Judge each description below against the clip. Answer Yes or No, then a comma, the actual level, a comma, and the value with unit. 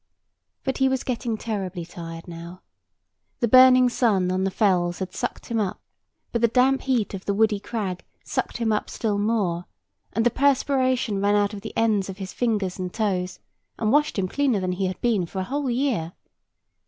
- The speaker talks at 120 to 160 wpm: No, average, 195 wpm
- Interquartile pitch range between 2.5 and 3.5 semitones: No, average, 4.6 semitones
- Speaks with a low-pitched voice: No, high, 210 Hz